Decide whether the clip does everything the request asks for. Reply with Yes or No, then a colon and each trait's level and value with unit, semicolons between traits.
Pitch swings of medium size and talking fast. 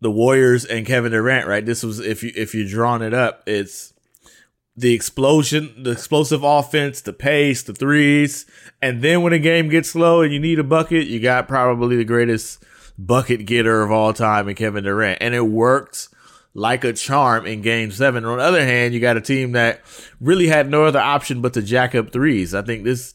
Yes: average, 4.0 semitones; fast, 215 wpm